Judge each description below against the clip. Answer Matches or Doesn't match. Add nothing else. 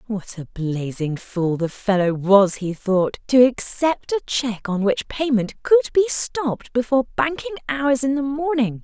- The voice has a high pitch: Matches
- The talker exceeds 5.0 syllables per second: Doesn't match